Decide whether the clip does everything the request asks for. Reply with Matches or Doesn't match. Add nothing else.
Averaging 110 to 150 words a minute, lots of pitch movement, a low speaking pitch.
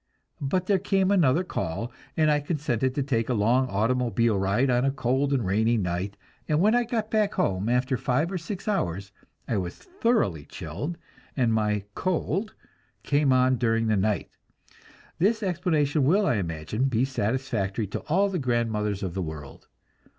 Doesn't match